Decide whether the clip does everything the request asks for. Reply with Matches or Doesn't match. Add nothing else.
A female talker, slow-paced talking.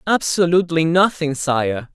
Doesn't match